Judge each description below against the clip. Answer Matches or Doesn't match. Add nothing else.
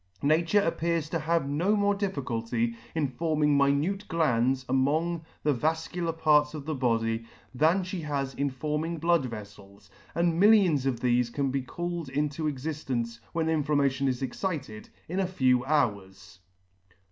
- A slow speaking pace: Doesn't match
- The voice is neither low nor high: Matches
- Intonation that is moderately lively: Matches